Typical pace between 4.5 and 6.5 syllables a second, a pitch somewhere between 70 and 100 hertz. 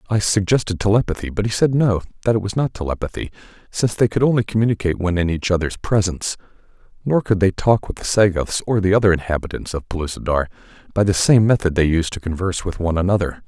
No: 6.7 syllables/s; very low, 95 Hz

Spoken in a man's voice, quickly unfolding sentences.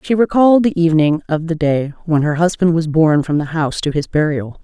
No: female; fast, 235 wpm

